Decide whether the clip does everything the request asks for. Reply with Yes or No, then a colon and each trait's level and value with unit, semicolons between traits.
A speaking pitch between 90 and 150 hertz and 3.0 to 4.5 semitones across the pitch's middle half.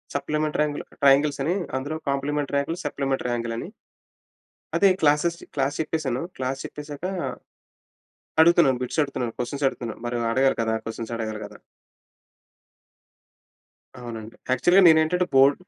Yes: medium, 140 Hz; average, 3.6 semitones